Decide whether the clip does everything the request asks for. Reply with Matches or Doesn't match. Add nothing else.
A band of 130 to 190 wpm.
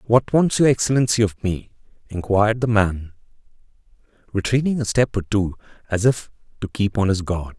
Matches